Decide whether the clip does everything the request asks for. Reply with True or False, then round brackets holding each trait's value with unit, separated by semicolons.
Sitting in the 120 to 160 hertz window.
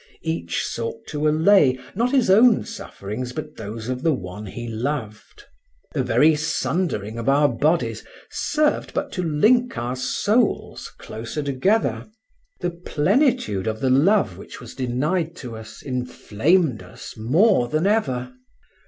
True (140 Hz)